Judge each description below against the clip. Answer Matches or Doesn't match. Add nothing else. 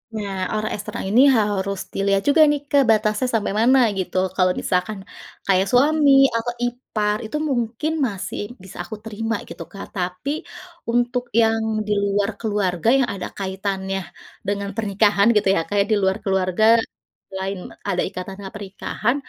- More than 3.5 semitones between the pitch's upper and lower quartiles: Doesn't match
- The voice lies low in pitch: Doesn't match